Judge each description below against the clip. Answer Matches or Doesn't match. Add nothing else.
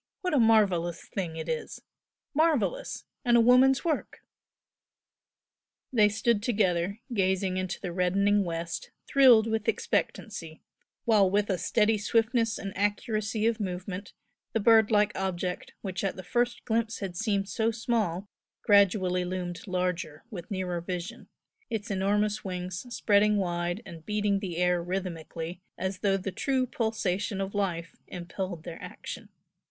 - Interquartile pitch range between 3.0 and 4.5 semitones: Matches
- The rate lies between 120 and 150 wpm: Matches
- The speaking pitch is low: Doesn't match